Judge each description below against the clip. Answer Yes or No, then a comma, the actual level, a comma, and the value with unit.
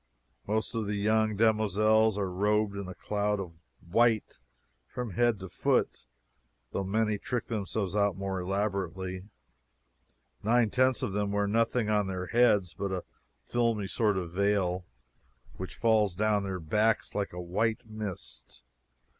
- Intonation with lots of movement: No, narrow, 2.4 semitones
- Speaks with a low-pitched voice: Yes, low, 105 Hz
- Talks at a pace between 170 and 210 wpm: No, average, 145 wpm